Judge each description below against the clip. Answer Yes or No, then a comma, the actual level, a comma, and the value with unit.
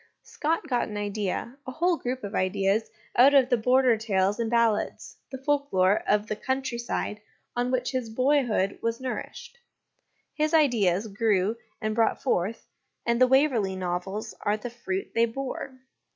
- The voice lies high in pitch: Yes, high, 235 Hz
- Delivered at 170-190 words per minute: No, average, 160 wpm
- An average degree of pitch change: Yes, average, 4.0 semitones